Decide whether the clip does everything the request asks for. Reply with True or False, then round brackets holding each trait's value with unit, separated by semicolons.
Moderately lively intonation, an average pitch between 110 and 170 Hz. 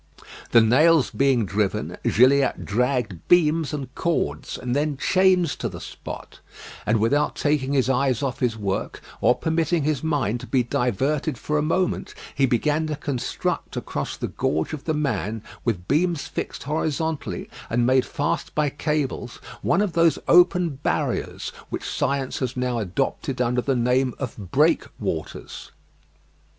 True (3.9 semitones; 135 Hz)